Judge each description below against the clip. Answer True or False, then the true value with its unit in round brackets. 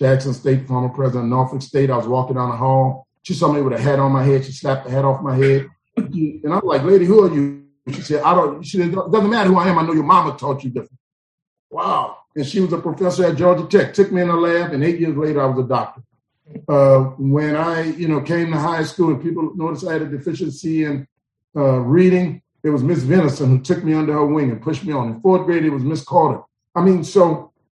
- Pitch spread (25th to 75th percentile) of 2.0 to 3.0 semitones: False (4.1 semitones)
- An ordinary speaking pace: False (260 wpm)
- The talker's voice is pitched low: False (150 Hz)